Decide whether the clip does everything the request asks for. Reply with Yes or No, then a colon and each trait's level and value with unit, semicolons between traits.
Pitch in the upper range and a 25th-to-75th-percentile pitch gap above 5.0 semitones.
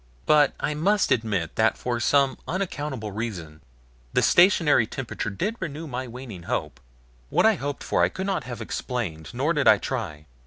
No: low, 130 Hz; wide, 5.6 semitones